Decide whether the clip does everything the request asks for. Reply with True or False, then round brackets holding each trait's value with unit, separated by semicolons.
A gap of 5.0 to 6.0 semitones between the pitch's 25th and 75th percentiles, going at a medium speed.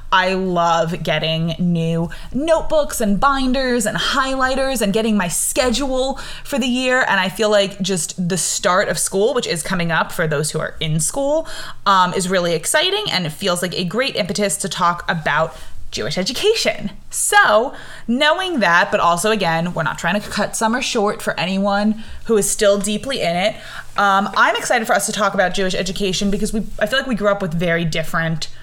True (5.4 semitones; 195 wpm)